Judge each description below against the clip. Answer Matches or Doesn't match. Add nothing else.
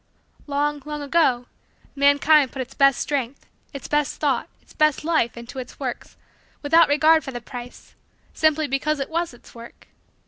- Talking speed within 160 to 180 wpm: Matches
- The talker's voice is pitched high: Matches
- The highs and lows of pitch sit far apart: Doesn't match